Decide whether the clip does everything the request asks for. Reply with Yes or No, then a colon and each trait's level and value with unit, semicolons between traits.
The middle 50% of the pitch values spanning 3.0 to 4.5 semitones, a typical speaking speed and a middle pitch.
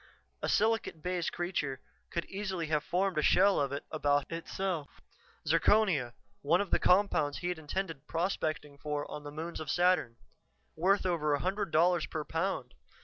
Yes: average, 3.9 semitones; average, 160 wpm; medium, 165 Hz